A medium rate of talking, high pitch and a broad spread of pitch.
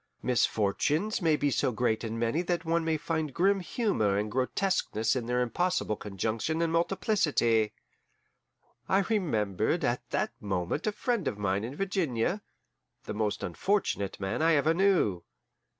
No: average, 150 wpm; medium, 145 Hz; wide, 8.6 semitones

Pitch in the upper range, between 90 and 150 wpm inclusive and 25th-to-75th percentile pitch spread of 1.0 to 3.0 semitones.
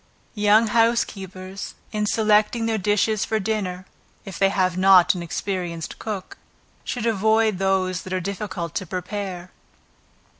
Yes: high, 195 Hz; slow, 135 wpm; narrow, 2.6 semitones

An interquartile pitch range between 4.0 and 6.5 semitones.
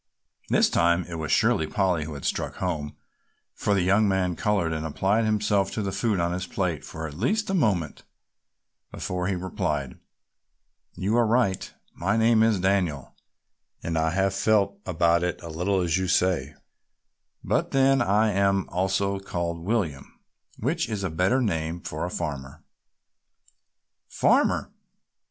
No: average, 3.5 semitones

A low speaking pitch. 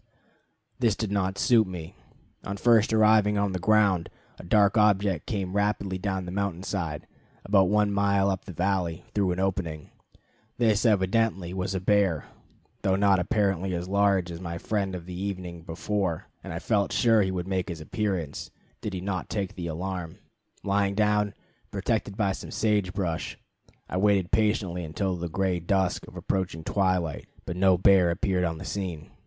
Yes: very low, 95 Hz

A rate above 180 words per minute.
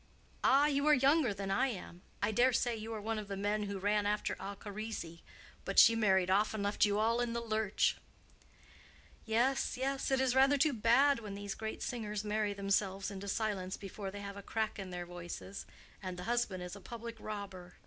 Yes: average, 200 wpm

